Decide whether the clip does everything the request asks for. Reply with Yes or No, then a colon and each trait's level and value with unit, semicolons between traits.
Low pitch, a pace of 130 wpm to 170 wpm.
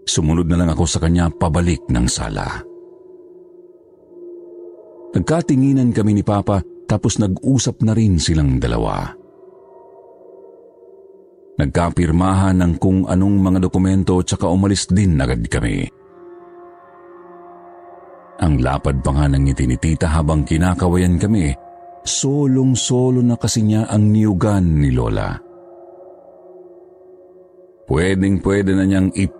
No: low, 105 Hz; slow, 110 wpm